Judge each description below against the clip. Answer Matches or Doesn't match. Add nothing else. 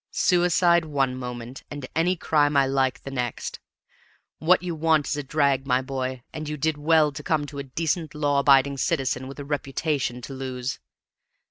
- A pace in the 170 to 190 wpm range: Matches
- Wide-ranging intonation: Doesn't match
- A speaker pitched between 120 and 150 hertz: Matches